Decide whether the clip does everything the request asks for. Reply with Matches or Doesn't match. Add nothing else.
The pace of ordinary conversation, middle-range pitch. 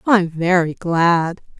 Matches